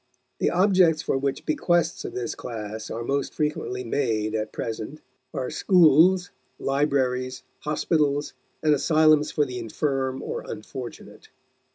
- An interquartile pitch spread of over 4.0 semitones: No, average, 3.7 semitones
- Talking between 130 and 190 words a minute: Yes, slow, 135 wpm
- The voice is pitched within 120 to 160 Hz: Yes, medium, 140 Hz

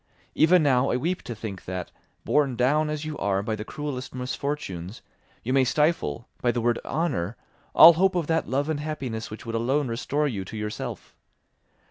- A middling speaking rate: Yes, average, 185 wpm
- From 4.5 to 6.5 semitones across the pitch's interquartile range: Yes, average, 5.2 semitones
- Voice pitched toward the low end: Yes, low, 130 Hz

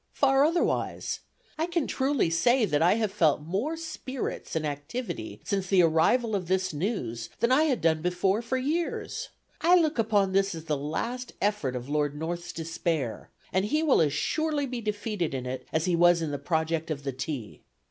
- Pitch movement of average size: No, wide, 8.0 semitones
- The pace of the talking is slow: No, average, 190 wpm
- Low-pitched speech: No, medium, 185 Hz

